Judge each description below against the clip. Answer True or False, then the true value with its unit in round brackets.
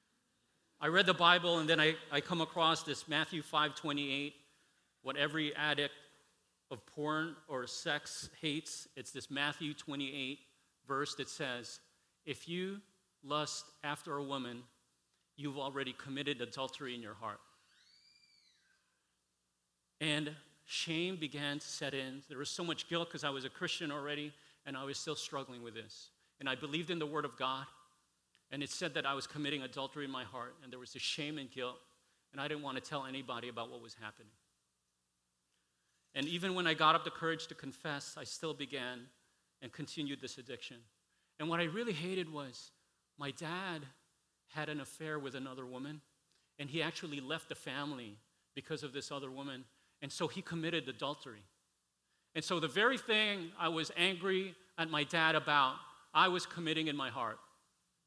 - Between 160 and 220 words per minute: True (175 wpm)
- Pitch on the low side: False (145 Hz)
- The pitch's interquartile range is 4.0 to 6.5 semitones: False (3.3 semitones)